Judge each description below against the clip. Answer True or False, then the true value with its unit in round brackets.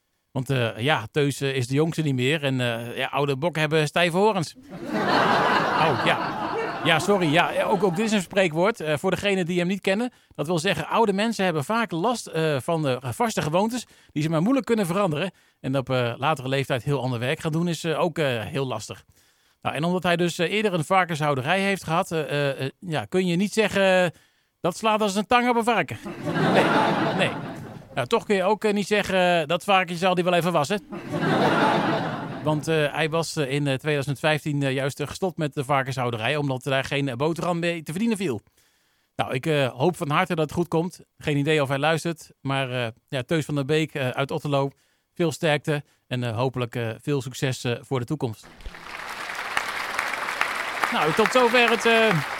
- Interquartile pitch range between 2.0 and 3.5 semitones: False (5.1 semitones)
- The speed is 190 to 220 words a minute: True (195 wpm)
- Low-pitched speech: False (155 Hz)